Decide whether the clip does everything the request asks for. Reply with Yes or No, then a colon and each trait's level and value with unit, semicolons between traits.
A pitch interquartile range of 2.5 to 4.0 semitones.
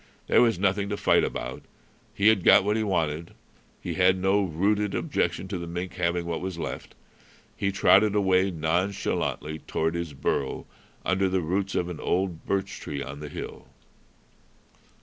Yes: average, 2.8 semitones